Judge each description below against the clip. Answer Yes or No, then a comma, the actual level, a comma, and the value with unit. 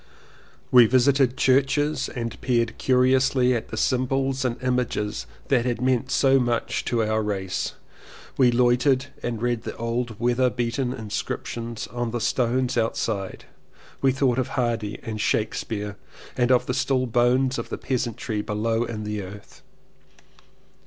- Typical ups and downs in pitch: No, narrow, 2.2 semitones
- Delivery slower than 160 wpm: Yes, average, 145 wpm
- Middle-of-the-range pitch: No, low, 120 Hz